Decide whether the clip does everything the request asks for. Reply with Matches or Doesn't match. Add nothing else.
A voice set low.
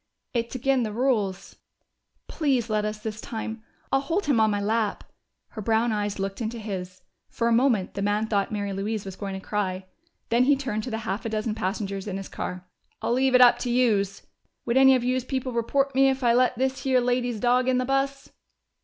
Doesn't match